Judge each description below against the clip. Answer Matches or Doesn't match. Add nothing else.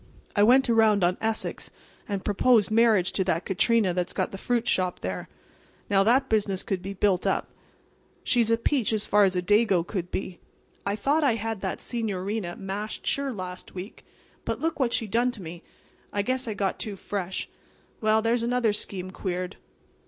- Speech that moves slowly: Doesn't match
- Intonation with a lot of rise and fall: Doesn't match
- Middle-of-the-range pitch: Doesn't match